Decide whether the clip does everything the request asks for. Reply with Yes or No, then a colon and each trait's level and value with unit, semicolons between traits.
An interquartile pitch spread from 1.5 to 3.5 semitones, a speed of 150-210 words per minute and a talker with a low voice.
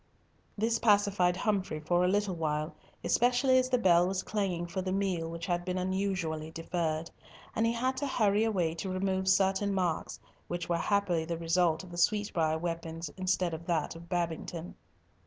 No: average, 3.1 semitones; average, 175 wpm; medium, 180 Hz